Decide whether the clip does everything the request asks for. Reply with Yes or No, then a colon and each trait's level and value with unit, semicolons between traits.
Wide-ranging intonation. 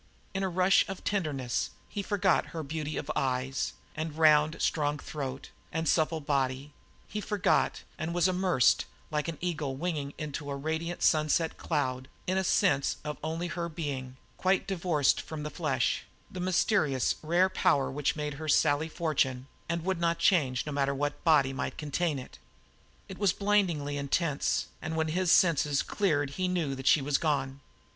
No: average, 3.6 semitones